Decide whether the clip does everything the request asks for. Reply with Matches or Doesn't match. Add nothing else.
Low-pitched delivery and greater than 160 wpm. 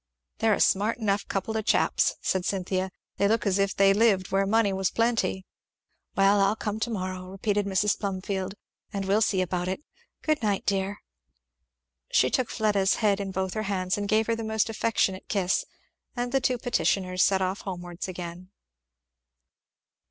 Doesn't match